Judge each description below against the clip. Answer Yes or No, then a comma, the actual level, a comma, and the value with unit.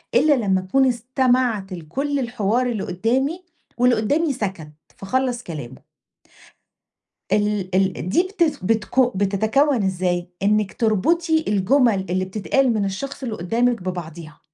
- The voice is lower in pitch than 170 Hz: No, high, 220 Hz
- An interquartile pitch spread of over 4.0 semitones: Yes, wide, 5.5 semitones